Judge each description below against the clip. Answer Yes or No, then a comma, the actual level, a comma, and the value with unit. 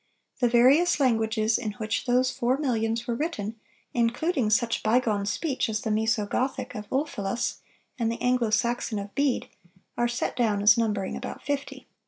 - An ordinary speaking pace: Yes, average, 165 wpm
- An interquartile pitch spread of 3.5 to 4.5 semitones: No, average, 2.7 semitones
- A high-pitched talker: Yes, high, 235 Hz